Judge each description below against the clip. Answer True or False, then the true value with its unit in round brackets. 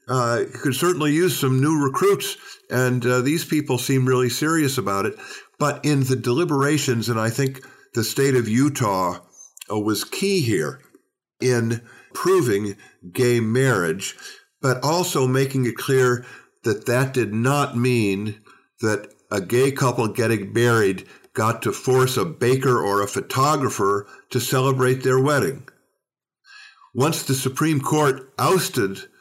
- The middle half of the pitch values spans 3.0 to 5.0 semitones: True (3.3 semitones)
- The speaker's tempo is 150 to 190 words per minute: False (140 wpm)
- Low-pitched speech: True (130 Hz)